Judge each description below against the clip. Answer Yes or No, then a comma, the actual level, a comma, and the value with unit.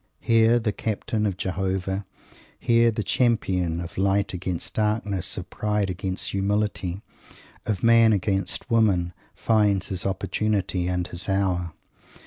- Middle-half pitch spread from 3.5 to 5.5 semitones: No, narrow, 2.6 semitones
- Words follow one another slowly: Yes, slow, 125 wpm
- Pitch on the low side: Yes, low, 100 Hz